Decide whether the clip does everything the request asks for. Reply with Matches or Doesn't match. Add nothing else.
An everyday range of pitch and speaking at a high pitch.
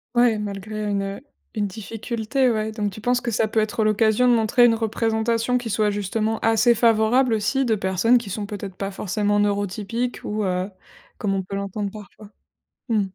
Doesn't match